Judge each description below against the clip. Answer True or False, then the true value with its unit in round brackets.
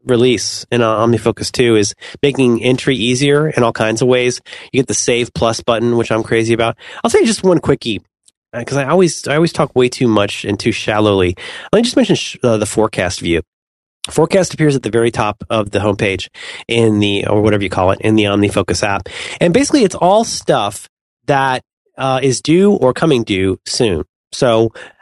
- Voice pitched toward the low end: True (115 Hz)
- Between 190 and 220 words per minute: True (200 wpm)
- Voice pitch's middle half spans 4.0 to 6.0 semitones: True (4.3 semitones)